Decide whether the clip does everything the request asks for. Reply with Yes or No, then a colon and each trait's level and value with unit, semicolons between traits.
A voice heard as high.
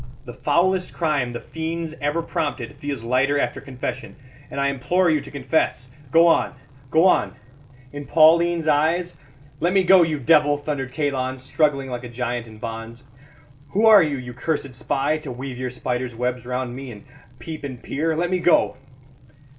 No: medium, 140 Hz